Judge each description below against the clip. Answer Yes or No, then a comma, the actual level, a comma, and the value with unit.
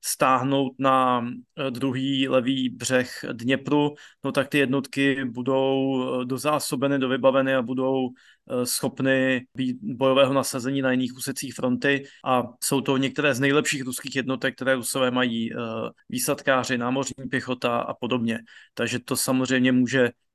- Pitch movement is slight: Yes, narrow, 1.3 semitones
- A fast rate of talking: No, average, 125 wpm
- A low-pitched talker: Yes, low, 130 Hz